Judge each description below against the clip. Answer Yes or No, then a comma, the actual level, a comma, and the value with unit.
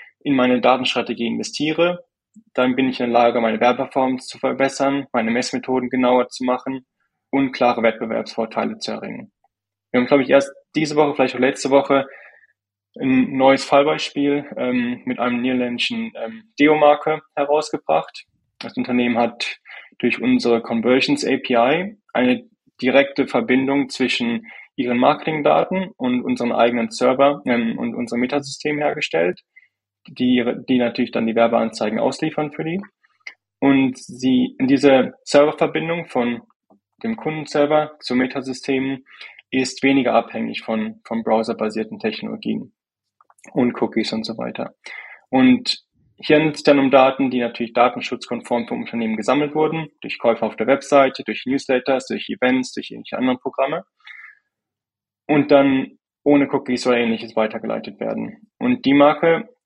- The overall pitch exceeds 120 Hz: Yes, low, 135 Hz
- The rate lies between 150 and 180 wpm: No, average, 135 wpm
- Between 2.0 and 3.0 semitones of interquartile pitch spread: No, average, 3.9 semitones